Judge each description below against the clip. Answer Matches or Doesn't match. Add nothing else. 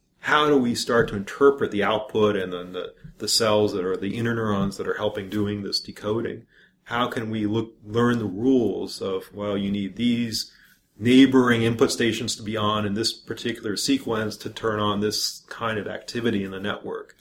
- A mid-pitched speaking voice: Doesn't match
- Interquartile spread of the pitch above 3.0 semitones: Doesn't match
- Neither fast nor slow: Matches